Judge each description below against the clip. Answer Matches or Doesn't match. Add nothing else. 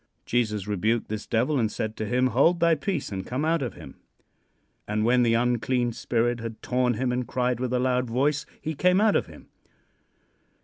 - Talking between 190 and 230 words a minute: Matches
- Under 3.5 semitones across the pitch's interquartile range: Matches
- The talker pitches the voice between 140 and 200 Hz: Doesn't match